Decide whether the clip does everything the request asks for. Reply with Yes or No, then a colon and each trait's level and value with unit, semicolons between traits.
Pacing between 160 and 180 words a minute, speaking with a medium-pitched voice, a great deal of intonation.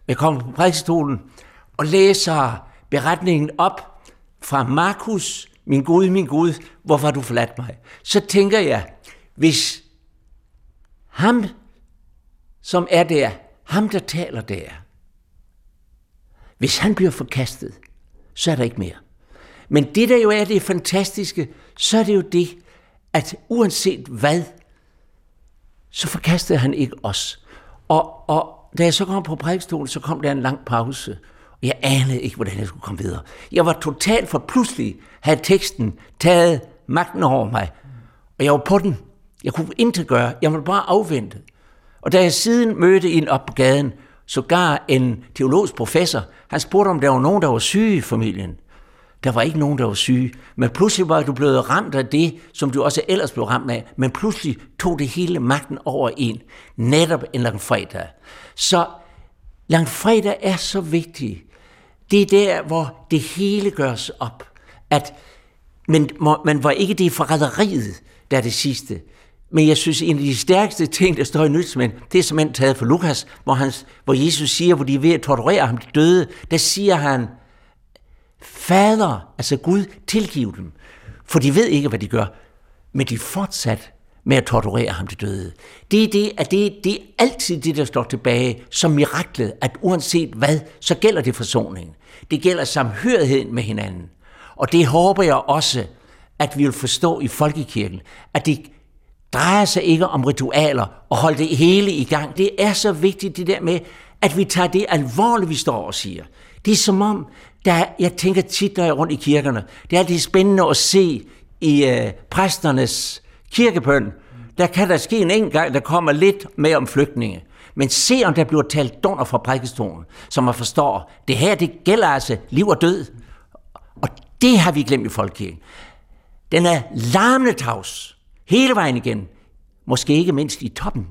Yes: average, 175 wpm; medium, 150 Hz; wide, 6.4 semitones